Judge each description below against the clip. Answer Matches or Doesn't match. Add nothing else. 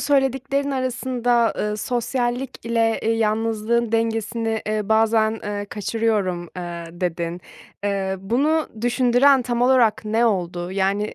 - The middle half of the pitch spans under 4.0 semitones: Matches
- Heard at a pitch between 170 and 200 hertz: Doesn't match